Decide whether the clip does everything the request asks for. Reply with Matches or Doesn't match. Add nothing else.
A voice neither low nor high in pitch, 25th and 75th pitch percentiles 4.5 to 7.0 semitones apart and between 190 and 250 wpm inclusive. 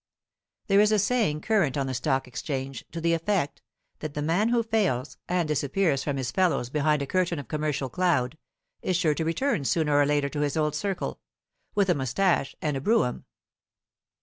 Matches